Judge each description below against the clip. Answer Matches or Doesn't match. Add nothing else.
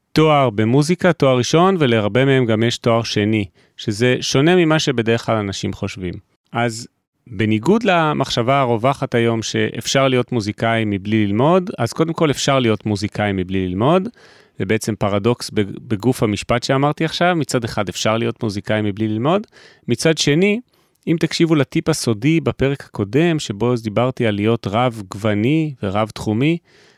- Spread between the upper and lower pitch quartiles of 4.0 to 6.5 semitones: Matches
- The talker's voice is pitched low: Matches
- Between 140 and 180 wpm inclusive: Matches